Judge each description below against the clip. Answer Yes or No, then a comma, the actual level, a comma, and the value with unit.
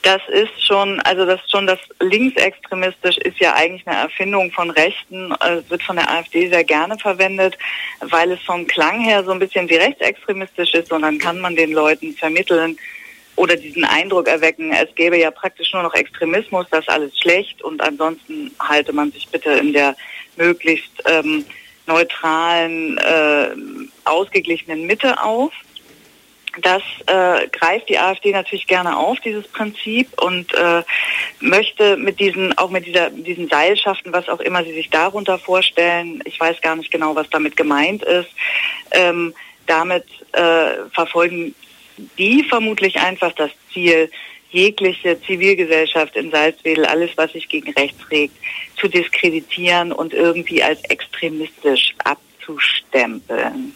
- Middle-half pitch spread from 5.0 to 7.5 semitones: No, average, 3.2 semitones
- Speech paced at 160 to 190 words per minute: No, average, 150 wpm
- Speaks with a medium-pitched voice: Yes, medium, 175 Hz